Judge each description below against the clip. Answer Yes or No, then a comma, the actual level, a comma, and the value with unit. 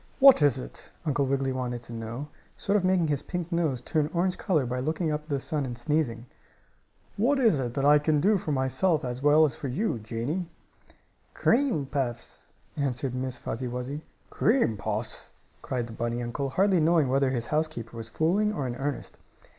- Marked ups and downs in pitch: No, average, 4.7 semitones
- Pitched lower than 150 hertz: Yes, medium, 140 Hz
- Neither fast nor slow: Yes, average, 190 wpm